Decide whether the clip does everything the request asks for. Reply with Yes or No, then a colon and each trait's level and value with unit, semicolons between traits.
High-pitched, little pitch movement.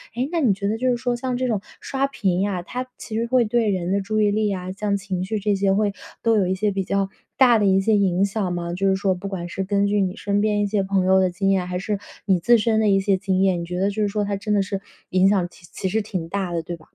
Yes: high, 200 Hz; narrow, 2.2 semitones